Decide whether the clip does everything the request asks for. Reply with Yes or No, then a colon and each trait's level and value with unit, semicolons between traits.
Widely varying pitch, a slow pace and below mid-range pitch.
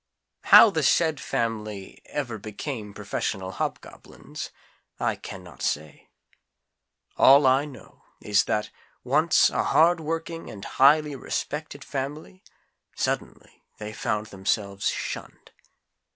Yes: wide, 6.5 semitones; slow, 110 wpm; low, 130 Hz